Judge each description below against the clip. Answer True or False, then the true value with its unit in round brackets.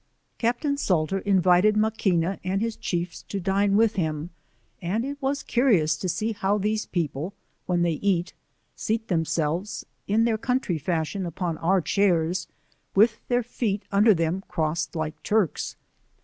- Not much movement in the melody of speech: False (4.2 semitones)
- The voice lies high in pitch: True (195 Hz)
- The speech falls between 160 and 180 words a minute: False (150 wpm)